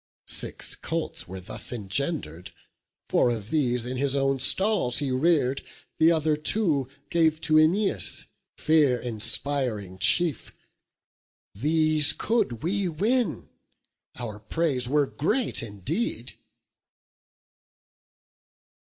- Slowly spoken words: Yes, slow, 100 wpm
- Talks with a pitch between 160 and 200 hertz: No, medium, 140 Hz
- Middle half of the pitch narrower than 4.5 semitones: No, average, 5.0 semitones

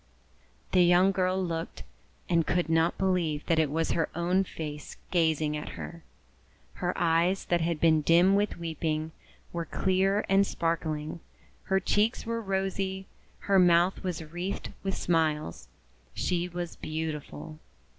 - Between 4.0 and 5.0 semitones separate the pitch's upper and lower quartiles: No, average, 2.8 semitones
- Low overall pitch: No, medium, 170 Hz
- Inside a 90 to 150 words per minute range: Yes, average, 140 wpm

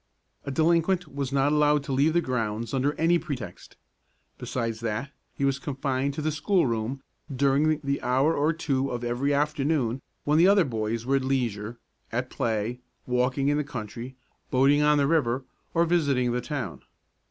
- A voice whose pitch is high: No, low, 135 Hz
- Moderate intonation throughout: Yes, average, 3.3 semitones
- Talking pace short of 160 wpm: No, average, 170 wpm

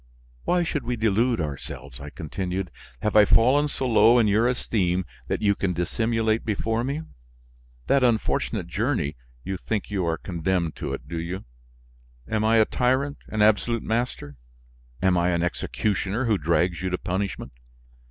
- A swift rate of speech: No, average, 160 wpm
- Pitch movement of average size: Yes, average, 4.6 semitones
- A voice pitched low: Yes, low, 105 Hz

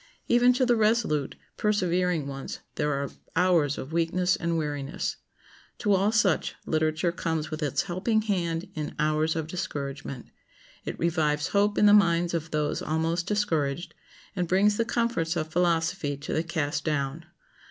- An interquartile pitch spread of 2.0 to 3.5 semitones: No, average, 3.9 semitones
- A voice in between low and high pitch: Yes, medium, 165 Hz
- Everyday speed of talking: Yes, average, 155 wpm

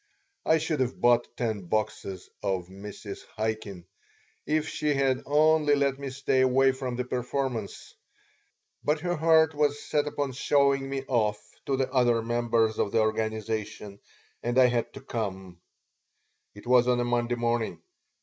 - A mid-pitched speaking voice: No, low, 125 Hz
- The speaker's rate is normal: Yes, average, 155 wpm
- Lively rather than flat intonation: No, average, 4.1 semitones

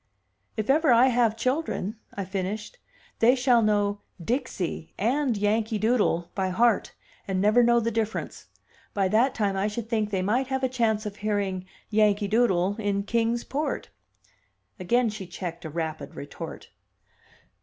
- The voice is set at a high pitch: Yes, high, 215 Hz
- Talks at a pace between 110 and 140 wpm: No, average, 155 wpm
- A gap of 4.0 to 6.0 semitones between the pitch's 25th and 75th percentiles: No, average, 3.4 semitones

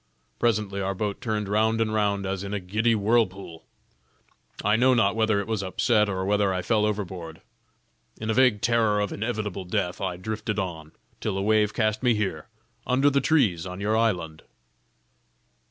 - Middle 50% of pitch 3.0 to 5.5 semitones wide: No, narrow, 2.4 semitones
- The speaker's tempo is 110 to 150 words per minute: No, average, 175 wpm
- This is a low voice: Yes, low, 105 Hz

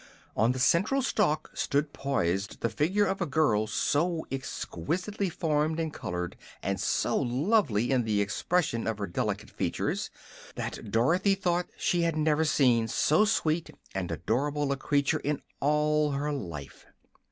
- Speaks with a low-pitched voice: No, medium, 145 Hz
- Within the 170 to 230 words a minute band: No, average, 150 wpm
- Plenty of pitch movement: Yes, wide, 6.4 semitones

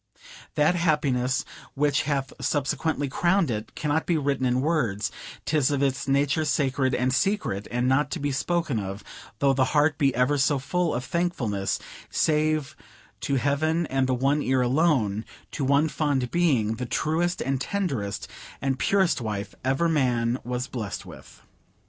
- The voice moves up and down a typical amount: Yes, average, 3.5 semitones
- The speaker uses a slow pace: No, average, 160 wpm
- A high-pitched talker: No, medium, 140 Hz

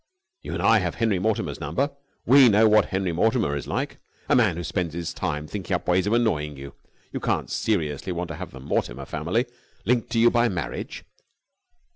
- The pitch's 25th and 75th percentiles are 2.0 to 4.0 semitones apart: No, wide, 5.6 semitones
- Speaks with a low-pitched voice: Yes, very low, 95 Hz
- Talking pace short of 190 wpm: No, average, 200 wpm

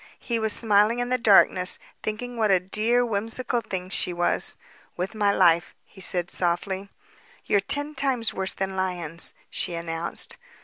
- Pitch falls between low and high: No, high, 200 Hz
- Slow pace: No, average, 160 wpm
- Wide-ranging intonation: No, average, 4.0 semitones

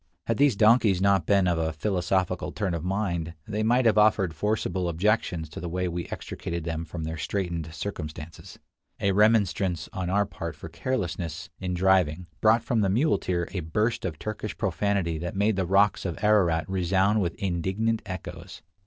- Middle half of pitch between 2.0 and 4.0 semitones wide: Yes, average, 3.7 semitones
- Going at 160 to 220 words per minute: Yes, average, 175 wpm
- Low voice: Yes, very low, 95 Hz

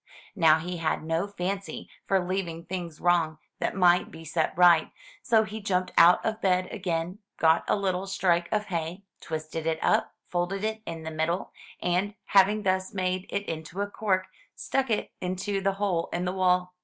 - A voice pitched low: No, medium, 180 Hz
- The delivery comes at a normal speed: Yes, average, 180 wpm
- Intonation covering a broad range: No, average, 2.7 semitones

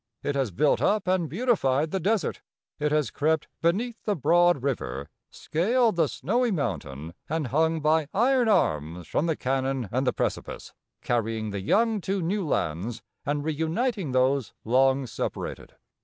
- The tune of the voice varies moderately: No, wide, 6.7 semitones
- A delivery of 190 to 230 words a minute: No, average, 155 wpm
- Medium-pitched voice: Yes, medium, 150 Hz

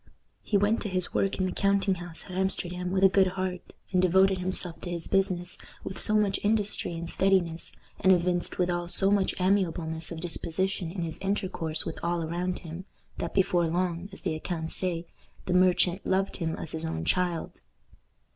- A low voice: No, medium, 180 Hz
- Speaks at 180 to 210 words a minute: Yes, average, 185 wpm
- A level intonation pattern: Yes, narrow, 2.0 semitones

